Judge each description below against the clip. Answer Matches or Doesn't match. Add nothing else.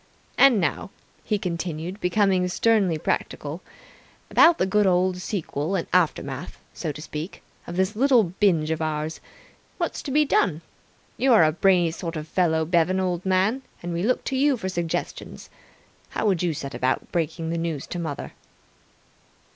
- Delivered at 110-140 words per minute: Doesn't match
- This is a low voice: Doesn't match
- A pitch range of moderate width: Matches